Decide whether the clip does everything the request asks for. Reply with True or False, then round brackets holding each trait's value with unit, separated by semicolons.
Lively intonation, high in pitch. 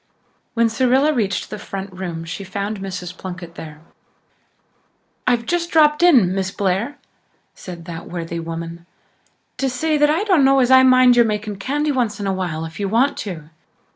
True (6.6 semitones; 205 Hz)